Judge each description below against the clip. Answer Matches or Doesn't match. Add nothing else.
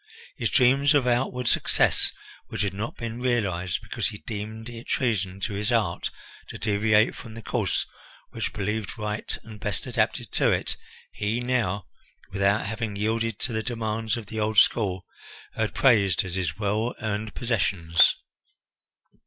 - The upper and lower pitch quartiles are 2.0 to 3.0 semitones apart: Matches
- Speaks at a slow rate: Doesn't match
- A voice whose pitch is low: Matches